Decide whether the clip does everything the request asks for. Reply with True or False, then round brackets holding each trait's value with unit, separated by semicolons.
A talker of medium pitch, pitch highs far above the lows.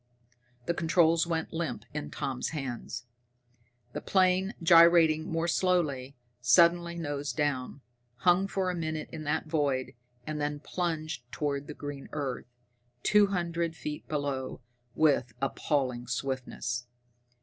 False (155 Hz; 3.8 semitones)